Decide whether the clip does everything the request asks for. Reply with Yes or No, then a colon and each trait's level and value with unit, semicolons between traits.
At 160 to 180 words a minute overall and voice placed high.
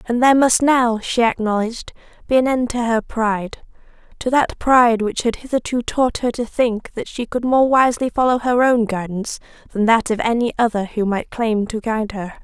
No: average, 200 wpm; high, 235 Hz